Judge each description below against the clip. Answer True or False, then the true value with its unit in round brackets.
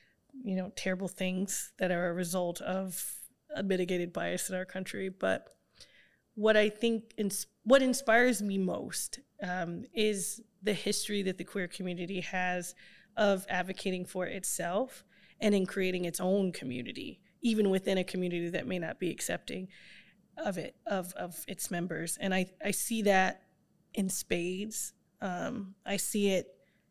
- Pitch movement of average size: False (2.0 semitones)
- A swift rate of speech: False (155 wpm)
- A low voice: False (190 Hz)